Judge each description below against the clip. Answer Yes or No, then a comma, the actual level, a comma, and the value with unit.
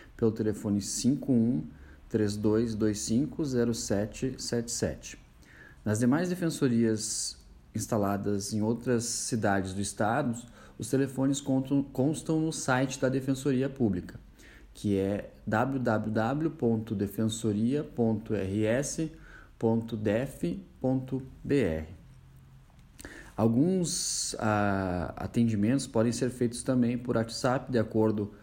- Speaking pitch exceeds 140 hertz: No, low, 115 Hz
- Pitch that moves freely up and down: No, average, 3.8 semitones